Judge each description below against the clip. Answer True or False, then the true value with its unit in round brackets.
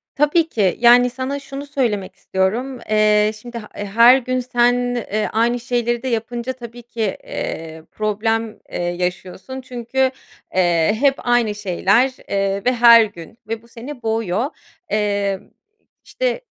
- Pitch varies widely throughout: False (3.2 semitones)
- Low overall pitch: False (230 Hz)